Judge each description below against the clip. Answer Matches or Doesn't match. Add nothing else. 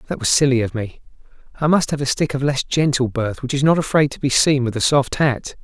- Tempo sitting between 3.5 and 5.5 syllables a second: Doesn't match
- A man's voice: Matches